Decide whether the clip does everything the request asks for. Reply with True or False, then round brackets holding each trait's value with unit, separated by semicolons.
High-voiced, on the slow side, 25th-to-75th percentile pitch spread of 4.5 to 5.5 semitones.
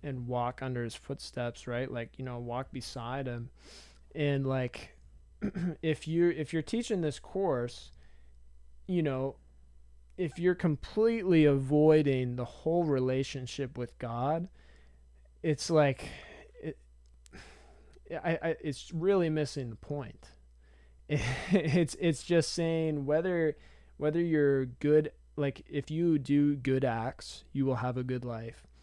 False (135 Hz; 130 wpm; 4.8 semitones)